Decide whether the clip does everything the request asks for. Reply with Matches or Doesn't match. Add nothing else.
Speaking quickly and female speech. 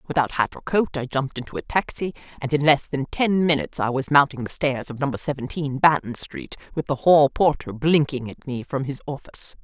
Matches